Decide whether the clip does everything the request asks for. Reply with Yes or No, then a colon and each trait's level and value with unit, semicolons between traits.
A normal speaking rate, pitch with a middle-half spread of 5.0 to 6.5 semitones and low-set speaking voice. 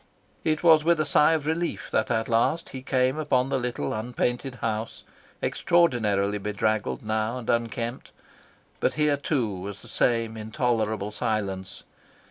No: average, 145 wpm; average, 4.4 semitones; low, 115 Hz